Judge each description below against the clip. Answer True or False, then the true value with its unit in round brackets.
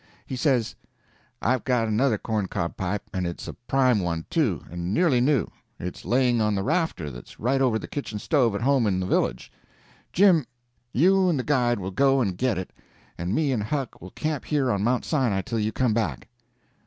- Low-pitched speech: True (120 Hz)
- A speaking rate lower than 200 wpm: False (205 wpm)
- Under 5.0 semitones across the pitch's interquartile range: False (5.6 semitones)